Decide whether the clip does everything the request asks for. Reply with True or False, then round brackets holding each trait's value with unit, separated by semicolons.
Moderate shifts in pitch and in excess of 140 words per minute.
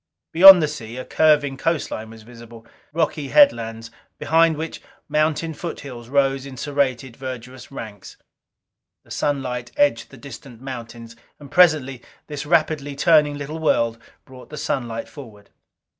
False (4.4 semitones; 135 wpm)